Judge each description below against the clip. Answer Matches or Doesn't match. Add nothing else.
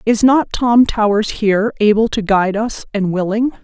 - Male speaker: Doesn't match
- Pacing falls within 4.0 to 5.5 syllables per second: Matches